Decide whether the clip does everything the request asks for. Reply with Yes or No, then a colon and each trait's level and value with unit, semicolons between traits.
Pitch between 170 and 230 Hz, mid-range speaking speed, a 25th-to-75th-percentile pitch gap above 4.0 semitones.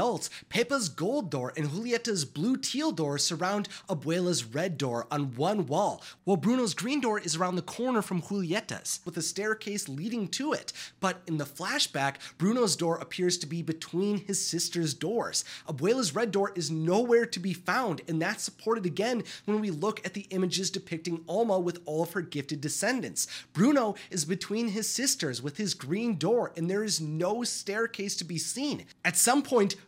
Yes: high, 190 Hz; average, 180 wpm; average, 4.7 semitones